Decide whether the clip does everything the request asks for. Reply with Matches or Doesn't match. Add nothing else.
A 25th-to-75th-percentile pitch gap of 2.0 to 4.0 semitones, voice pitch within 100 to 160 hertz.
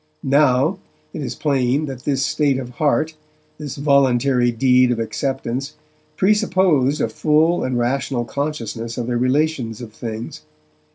Matches